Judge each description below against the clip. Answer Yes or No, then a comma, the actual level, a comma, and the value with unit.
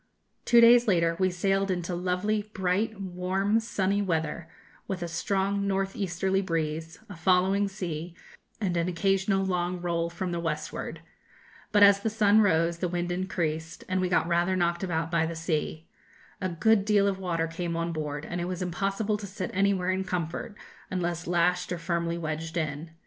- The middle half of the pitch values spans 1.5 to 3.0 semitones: Yes, narrow, 2.6 semitones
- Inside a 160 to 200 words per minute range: Yes, average, 175 wpm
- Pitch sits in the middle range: Yes, medium, 180 Hz